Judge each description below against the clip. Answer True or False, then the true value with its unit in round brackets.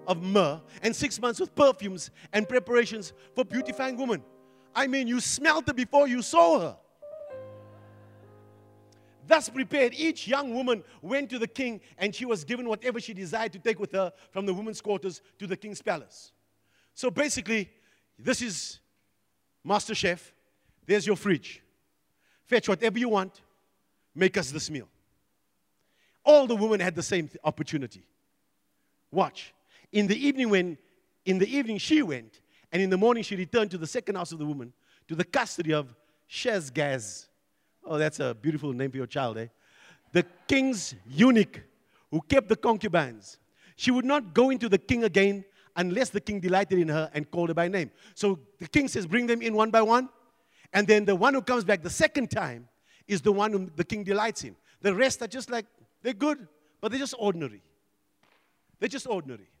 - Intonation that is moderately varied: False (7.9 semitones)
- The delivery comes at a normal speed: True (180 wpm)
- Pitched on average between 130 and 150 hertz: False (195 Hz)